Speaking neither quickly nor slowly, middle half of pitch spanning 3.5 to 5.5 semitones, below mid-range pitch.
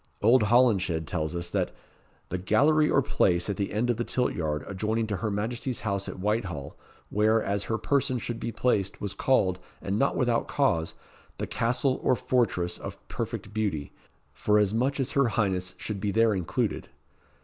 Yes: average, 180 wpm; average, 4.2 semitones; low, 105 Hz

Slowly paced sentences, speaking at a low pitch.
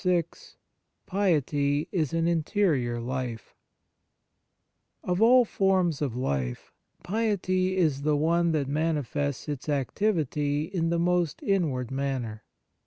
No: slow, 110 wpm; medium, 155 Hz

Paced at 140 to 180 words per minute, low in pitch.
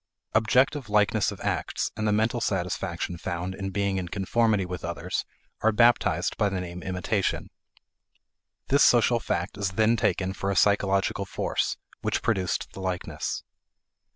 Yes: average, 150 wpm; low, 100 Hz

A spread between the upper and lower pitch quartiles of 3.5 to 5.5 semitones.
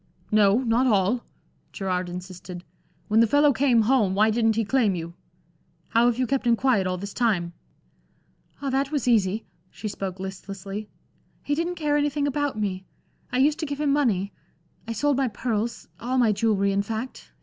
Yes: average, 5.1 semitones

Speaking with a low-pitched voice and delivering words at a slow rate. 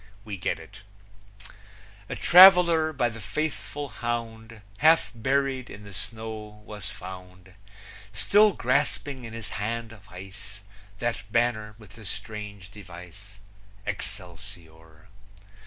Yes: low, 105 Hz; slow, 115 wpm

